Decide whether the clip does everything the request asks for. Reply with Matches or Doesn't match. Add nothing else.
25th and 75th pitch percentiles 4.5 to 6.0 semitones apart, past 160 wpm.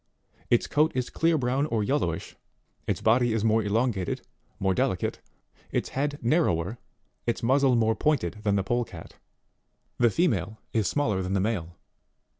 Doesn't match